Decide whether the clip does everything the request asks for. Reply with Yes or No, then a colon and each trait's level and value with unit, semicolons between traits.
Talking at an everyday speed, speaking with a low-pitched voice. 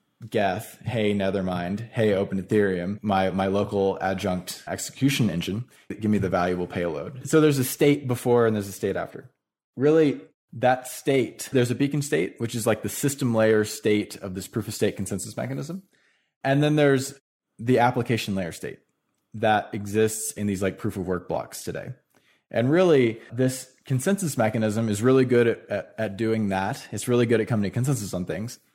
Yes: average, 180 wpm; low, 110 Hz